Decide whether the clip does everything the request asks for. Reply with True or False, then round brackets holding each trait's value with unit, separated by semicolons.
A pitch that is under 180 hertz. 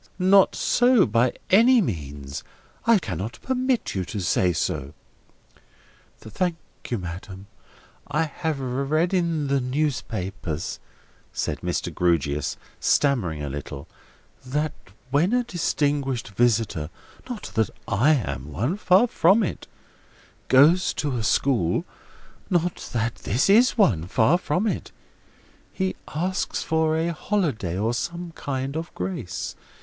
True (135 Hz)